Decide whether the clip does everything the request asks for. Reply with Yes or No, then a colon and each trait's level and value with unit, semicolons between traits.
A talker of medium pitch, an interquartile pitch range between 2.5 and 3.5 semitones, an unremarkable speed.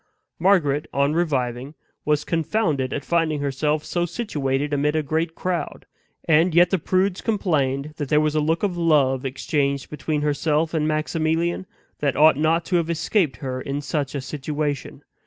Yes: medium, 150 Hz; average, 2.8 semitones; average, 165 wpm